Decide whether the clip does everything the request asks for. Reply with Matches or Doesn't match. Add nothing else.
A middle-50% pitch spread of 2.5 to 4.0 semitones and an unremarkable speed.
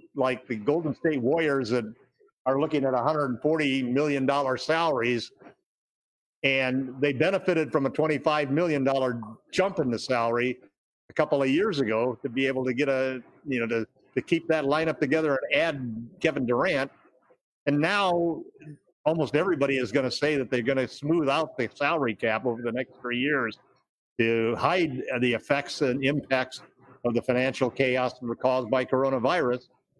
Matches